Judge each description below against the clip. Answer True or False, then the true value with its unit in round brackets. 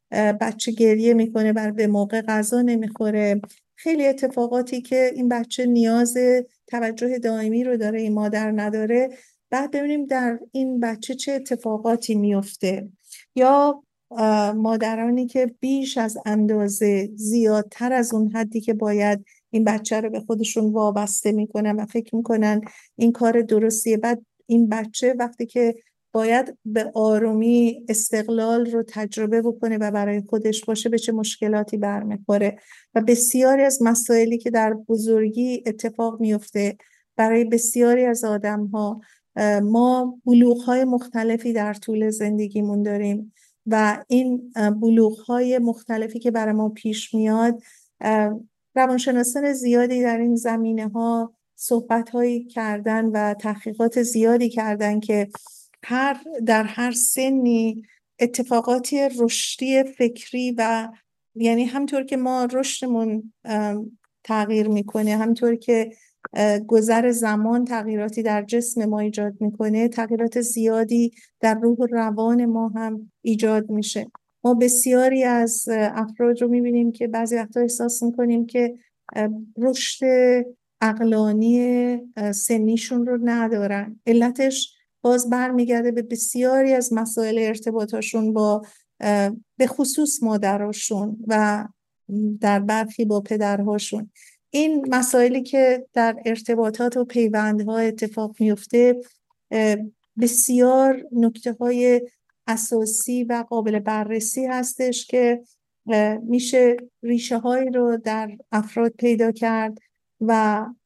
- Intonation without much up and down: True (2.0 semitones)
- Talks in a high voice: True (230 Hz)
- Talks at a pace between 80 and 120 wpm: True (115 wpm)